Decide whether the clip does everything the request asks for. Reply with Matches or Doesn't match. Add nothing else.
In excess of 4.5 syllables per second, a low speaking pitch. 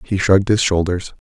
Matches